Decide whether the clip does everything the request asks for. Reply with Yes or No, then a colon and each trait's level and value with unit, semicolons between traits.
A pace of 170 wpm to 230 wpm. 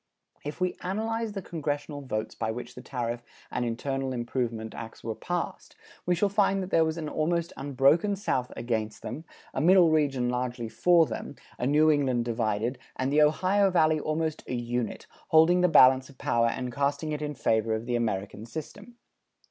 Yes: average, 180 wpm